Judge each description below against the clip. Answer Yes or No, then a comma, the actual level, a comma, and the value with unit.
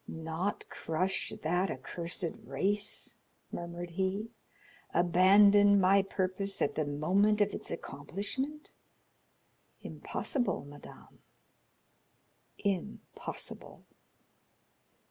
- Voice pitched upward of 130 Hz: Yes, high, 190 Hz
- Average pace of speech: No, slow, 75 wpm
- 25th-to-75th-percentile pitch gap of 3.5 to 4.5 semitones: No, average, 3.0 semitones